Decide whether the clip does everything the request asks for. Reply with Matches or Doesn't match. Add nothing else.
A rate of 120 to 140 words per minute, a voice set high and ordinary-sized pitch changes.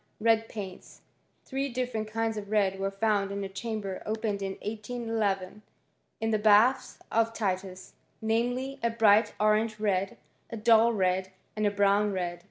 Doesn't match